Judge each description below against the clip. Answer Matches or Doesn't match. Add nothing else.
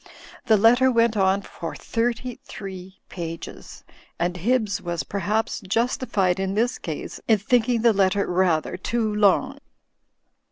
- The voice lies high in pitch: Matches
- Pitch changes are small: Doesn't match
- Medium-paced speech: Doesn't match